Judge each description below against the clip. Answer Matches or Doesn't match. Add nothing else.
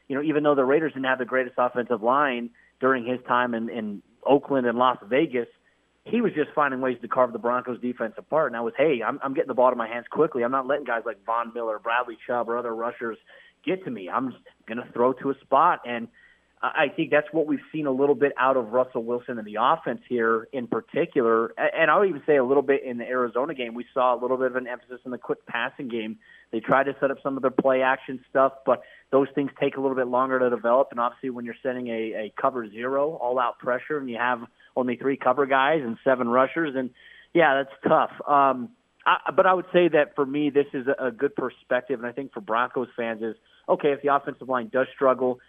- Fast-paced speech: Matches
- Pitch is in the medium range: Doesn't match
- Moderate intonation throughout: Doesn't match